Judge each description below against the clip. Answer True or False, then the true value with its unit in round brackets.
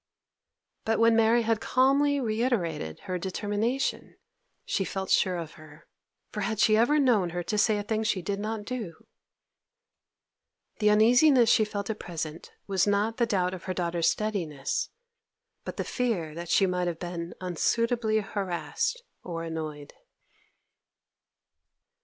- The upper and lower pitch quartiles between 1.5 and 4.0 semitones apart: False (4.5 semitones)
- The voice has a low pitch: False (205 Hz)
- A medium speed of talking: True (145 wpm)